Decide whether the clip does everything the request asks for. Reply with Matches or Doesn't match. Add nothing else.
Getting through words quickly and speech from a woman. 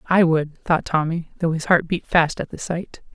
Matches